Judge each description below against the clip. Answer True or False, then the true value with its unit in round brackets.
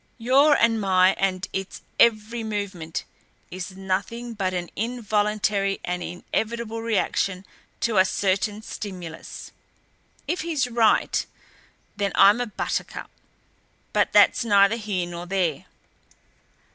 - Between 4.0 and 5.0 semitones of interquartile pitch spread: False (3.5 semitones)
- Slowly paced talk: True (115 wpm)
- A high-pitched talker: True (205 Hz)